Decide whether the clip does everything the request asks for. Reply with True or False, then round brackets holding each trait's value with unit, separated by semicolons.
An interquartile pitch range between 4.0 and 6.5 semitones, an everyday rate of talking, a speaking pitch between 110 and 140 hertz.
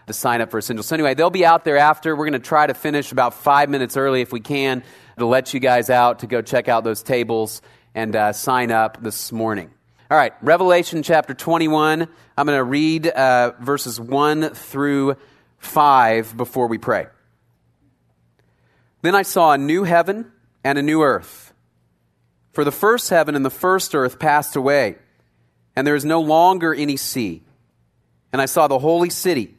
True (5.3 semitones; 185 wpm; 135 Hz)